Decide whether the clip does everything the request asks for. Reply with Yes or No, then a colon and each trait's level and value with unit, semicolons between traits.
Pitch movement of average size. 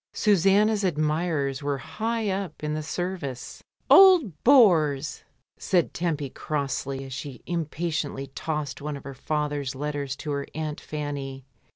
Yes: average, 4.0 semitones